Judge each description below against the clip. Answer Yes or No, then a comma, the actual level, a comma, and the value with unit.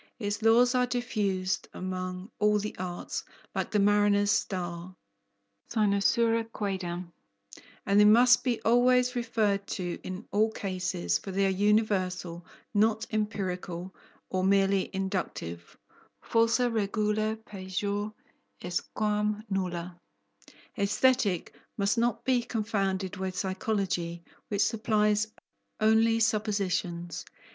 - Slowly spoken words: Yes, slow, 110 wpm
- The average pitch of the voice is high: Yes, high, 205 Hz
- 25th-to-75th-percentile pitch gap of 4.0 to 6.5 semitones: No, average, 3.0 semitones